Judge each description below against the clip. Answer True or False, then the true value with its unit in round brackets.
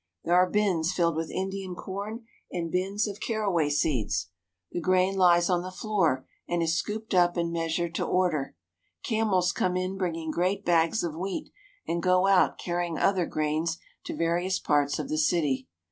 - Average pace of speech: True (175 wpm)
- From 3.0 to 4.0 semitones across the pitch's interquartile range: False (2.5 semitones)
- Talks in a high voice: False (175 Hz)